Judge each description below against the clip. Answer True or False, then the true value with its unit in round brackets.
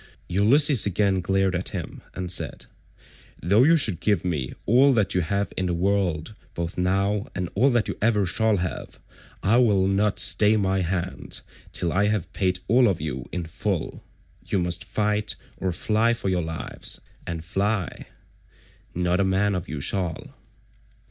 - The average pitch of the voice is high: False (95 Hz)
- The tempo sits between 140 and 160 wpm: False (170 wpm)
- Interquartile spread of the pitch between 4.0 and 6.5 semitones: False (2.9 semitones)